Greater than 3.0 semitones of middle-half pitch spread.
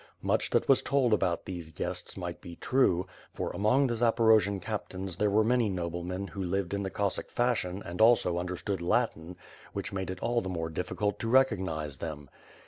Yes: average, 4.1 semitones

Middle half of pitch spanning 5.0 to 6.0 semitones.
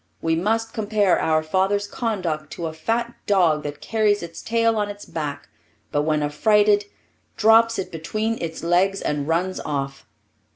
Yes: average, 5.3 semitones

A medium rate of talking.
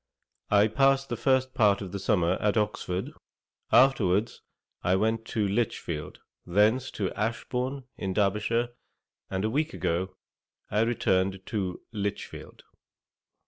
No: slow, 125 wpm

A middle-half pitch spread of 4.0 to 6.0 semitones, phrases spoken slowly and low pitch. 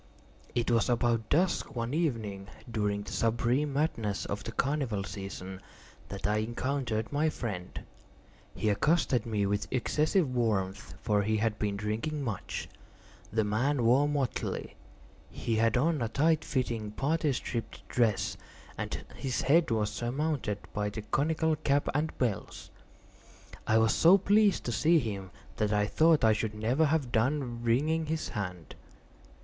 No: wide, 5.5 semitones; average, 150 wpm; low, 115 Hz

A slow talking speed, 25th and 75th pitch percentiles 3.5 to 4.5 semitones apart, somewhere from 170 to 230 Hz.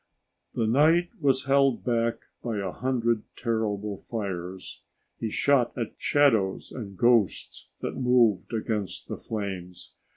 No: slow, 125 wpm; average, 4.1 semitones; low, 115 Hz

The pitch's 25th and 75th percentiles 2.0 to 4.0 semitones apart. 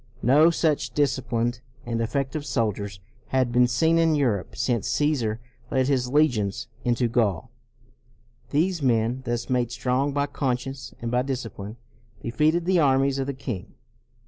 Yes: average, 3.4 semitones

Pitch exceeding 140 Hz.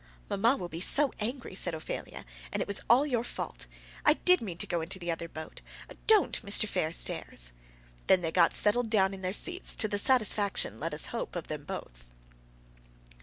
Yes: high, 190 Hz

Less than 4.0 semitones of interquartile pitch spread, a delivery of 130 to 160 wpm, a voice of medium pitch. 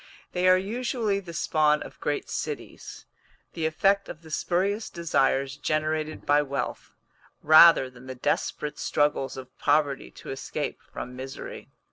No: average, 4.6 semitones; average, 140 wpm; medium, 155 Hz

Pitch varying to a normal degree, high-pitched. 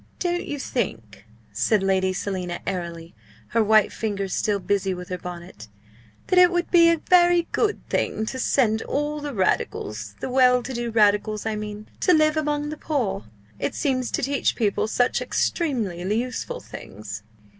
No: wide, 7.6 semitones; high, 220 Hz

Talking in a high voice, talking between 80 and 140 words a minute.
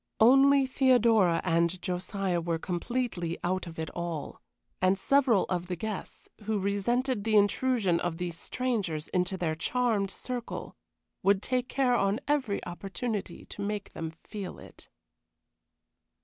Yes: high, 200 Hz; slow, 135 wpm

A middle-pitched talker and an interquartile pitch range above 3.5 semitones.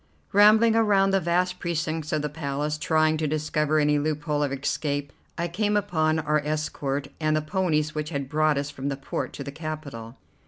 No: medium, 155 Hz; narrow, 2.4 semitones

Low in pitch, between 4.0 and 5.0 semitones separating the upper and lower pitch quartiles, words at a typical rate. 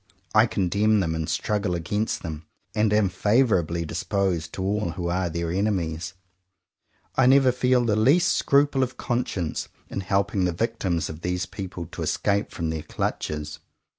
Yes: very low, 95 Hz; average, 4.3 semitones; average, 160 wpm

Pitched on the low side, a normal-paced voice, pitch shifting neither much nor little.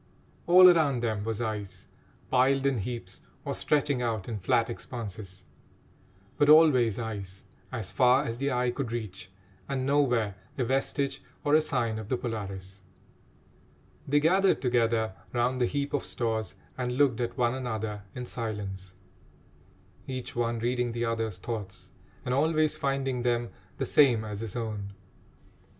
Yes: low, 120 Hz; average, 150 wpm; average, 3.6 semitones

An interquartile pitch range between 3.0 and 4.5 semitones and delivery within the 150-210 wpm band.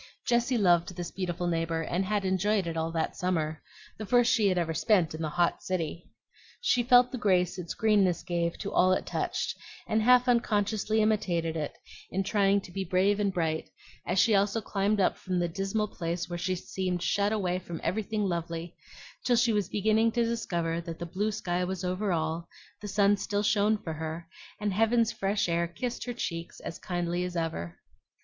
Yes: average, 3.7 semitones; average, 195 wpm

